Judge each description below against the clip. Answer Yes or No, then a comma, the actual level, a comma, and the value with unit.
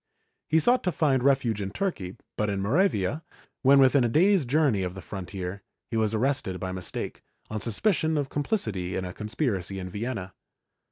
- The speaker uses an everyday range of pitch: No, wide, 7.1 semitones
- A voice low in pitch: Yes, low, 115 Hz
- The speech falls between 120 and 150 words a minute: No, average, 175 wpm